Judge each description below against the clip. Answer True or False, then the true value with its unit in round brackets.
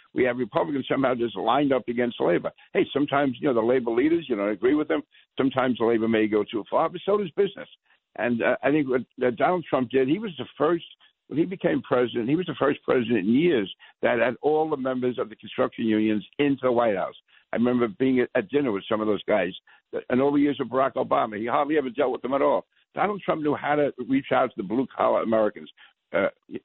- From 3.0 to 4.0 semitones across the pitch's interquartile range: True (3.4 semitones)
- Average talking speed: False (245 wpm)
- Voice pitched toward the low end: True (130 Hz)